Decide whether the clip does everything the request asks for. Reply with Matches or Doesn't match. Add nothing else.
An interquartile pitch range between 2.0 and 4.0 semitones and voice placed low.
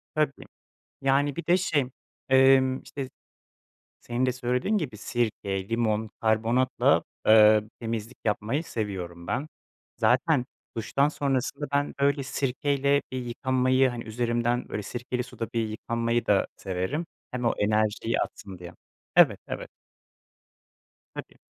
Matches